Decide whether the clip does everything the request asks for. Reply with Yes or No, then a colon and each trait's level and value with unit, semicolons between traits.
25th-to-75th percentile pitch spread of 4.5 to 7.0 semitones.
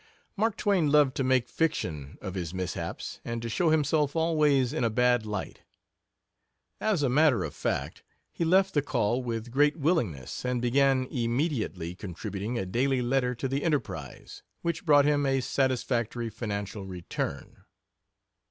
Yes: average, 5.2 semitones